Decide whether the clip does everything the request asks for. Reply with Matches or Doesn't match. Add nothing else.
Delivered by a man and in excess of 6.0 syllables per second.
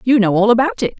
Doesn't match